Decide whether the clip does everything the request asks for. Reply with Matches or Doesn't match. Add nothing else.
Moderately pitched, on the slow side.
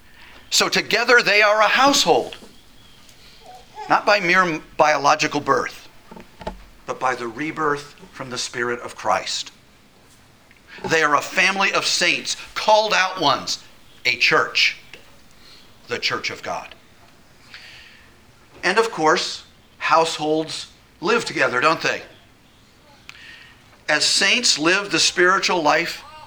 Matches